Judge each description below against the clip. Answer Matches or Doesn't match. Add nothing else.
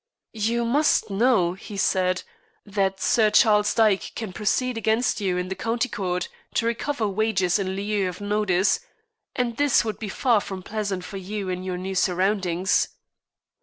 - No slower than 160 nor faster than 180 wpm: Matches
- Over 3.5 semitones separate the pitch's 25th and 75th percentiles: Doesn't match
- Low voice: Doesn't match